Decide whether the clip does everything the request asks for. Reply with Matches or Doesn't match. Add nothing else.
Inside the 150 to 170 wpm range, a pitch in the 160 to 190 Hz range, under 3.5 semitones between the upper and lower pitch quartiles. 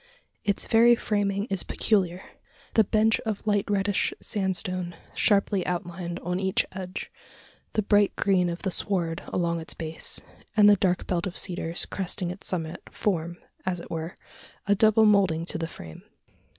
Matches